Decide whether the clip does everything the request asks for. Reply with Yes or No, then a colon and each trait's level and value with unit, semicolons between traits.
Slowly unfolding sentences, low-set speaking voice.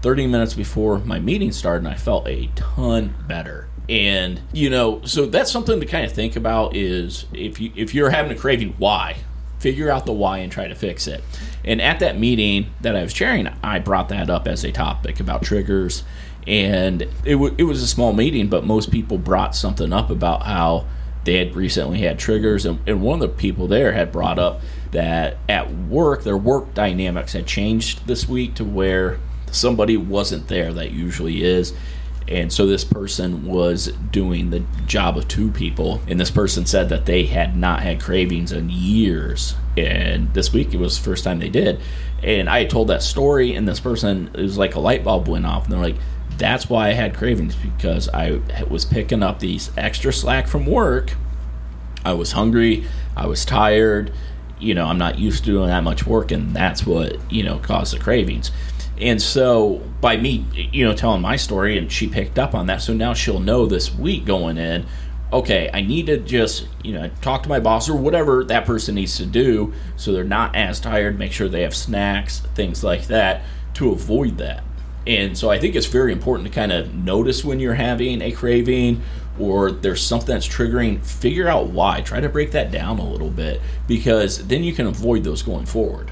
No: fast, 205 wpm; very low, 90 Hz